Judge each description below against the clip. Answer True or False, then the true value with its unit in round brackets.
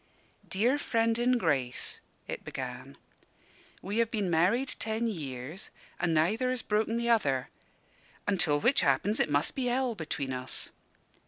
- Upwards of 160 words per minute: False (145 wpm)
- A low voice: False (205 Hz)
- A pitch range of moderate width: False (8.1 semitones)